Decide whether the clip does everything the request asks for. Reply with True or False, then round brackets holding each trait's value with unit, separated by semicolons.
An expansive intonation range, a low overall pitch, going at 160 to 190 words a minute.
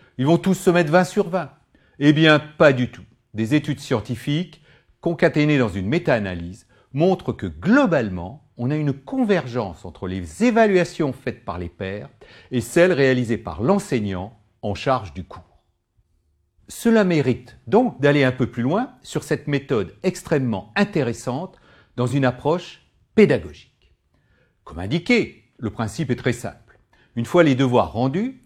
False (7.2 semitones; 130 Hz; 150 wpm)